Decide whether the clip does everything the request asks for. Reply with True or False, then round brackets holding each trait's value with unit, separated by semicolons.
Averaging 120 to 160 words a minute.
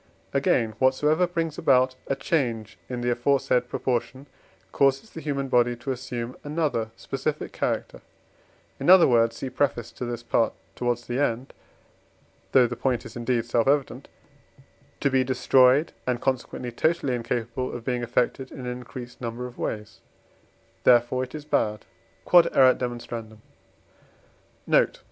True (140 wpm)